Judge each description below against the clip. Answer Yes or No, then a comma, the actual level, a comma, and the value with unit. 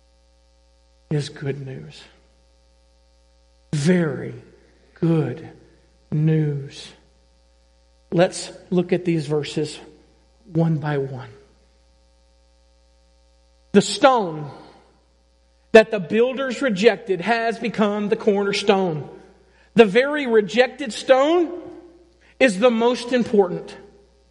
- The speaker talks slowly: Yes, slow, 80 wpm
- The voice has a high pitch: No, medium, 160 Hz